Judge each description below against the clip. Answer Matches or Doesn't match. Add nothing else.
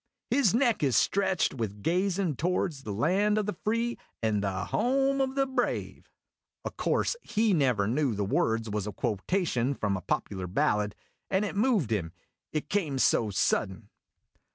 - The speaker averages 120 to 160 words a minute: Doesn't match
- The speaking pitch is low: Doesn't match